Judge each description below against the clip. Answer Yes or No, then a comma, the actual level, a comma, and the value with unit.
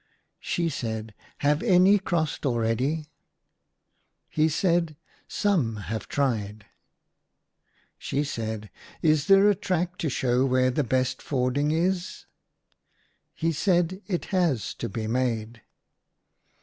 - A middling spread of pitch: No, wide, 6.6 semitones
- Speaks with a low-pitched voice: No, medium, 145 Hz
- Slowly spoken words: Yes, slow, 125 wpm